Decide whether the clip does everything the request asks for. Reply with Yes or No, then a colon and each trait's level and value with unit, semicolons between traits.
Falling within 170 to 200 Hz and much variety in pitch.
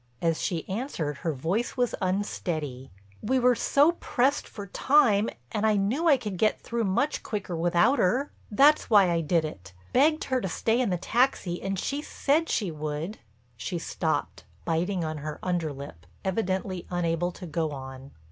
Yes: medium, 185 Hz; wide, 6.8 semitones